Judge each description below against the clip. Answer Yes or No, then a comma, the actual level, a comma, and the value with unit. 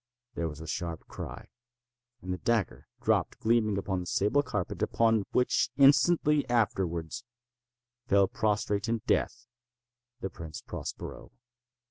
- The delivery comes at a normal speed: No, slow, 120 wpm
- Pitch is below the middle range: Yes, low, 110 Hz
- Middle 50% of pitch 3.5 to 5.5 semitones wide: Yes, average, 4.8 semitones